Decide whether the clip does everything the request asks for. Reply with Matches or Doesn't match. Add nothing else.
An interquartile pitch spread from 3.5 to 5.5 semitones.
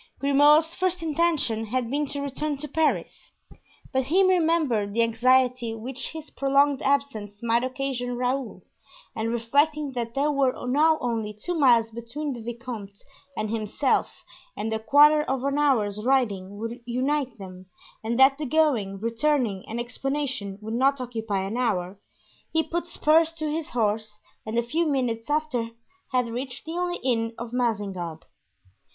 Matches